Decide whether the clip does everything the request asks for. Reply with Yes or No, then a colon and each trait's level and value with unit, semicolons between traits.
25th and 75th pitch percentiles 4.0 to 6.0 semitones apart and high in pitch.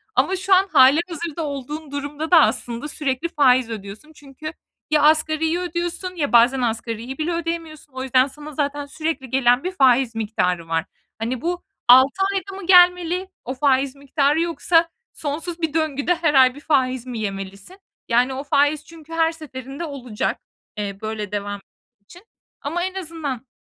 Yes: average, 4.4 semitones; very high, 285 Hz